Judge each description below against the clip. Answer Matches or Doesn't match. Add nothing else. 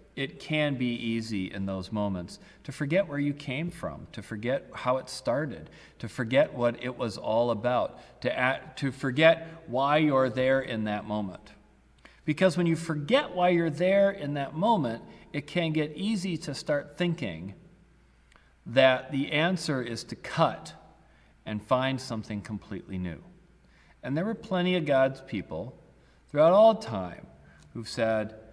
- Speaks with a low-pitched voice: Matches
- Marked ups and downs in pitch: Matches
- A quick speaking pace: Doesn't match